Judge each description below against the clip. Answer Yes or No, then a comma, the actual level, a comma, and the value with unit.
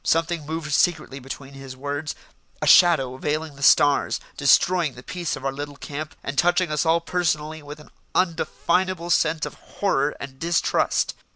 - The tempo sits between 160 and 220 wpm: Yes, average, 165 wpm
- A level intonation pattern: No, average, 3.2 semitones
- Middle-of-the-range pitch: Yes, medium, 155 Hz